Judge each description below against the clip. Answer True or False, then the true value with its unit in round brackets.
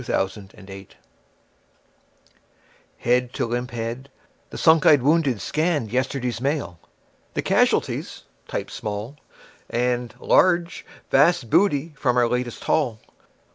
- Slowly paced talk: True (115 wpm)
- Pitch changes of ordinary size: True (4.1 semitones)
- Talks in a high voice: False (125 Hz)